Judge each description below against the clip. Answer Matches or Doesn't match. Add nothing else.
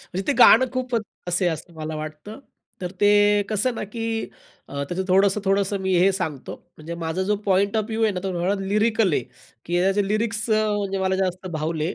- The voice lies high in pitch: Matches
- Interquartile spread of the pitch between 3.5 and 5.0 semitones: Doesn't match